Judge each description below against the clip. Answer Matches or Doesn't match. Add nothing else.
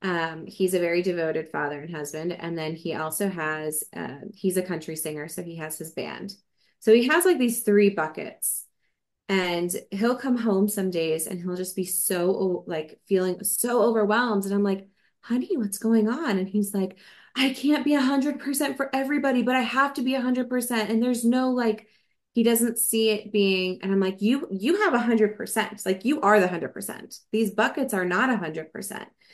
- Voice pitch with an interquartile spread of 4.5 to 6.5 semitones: Matches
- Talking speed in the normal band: Doesn't match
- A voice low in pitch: Doesn't match